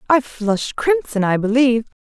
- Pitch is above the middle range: Yes, high, 245 Hz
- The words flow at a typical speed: Yes, average, 150 wpm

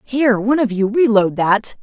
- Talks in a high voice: Yes, high, 225 Hz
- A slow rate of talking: No, average, 200 wpm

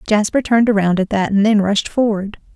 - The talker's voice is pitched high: Yes, high, 210 Hz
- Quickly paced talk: No, average, 190 wpm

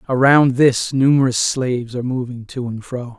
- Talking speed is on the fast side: No, average, 170 wpm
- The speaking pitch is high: No, low, 125 Hz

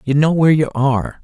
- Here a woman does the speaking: No, male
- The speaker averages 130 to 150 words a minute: No, fast, 245 wpm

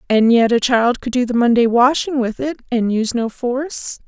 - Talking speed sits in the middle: No, fast, 220 wpm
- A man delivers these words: No, female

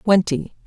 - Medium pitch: Yes, medium, 180 Hz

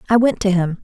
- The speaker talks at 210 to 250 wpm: No, fast, 285 wpm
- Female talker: Yes, female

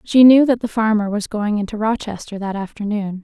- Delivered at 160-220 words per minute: Yes, fast, 205 wpm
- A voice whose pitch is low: No, high, 215 Hz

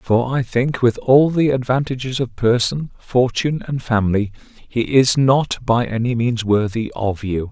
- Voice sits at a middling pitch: No, low, 120 Hz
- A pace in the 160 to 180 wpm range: Yes, average, 170 wpm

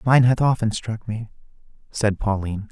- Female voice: No, male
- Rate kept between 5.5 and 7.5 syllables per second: No, 5.1 syllables/s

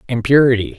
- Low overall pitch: Yes, low, 125 Hz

